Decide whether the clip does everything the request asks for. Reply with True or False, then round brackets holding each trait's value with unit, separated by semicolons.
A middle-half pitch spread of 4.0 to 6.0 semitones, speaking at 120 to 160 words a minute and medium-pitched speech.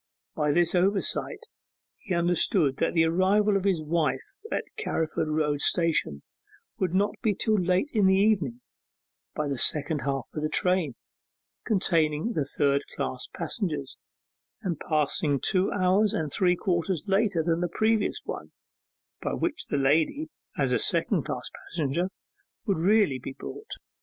True (4.5 semitones; 150 wpm; 170 Hz)